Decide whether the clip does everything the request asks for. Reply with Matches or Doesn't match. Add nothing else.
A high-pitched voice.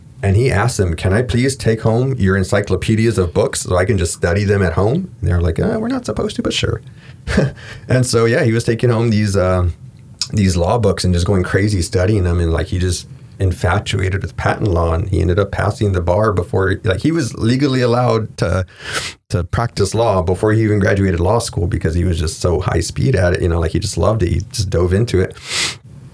Doesn't match